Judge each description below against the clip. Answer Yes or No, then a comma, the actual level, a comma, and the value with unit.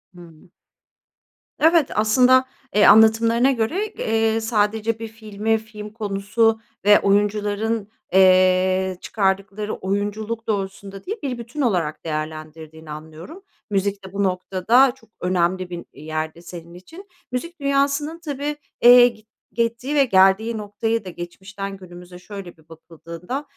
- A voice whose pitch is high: Yes, high, 205 Hz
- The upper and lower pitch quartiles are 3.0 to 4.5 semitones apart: Yes, average, 3.9 semitones